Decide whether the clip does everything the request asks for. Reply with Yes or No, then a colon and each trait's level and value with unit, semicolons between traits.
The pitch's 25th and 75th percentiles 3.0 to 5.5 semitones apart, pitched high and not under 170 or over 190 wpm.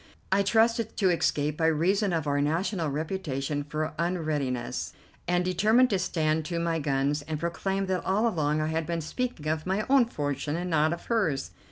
No: average, 4.2 semitones; medium, 165 Hz; average, 185 wpm